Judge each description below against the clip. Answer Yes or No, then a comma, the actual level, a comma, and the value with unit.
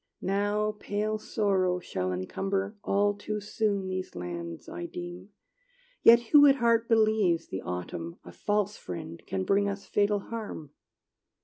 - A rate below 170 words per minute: Yes, average, 140 wpm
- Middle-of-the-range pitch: No, high, 200 Hz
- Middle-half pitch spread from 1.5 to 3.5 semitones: No, average, 4.3 semitones